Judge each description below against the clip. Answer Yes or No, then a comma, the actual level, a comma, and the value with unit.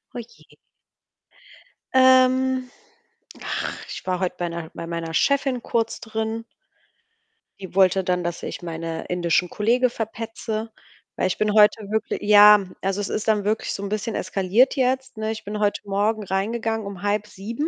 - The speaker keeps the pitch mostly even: No, average, 3.1 semitones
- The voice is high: Yes, high, 210 Hz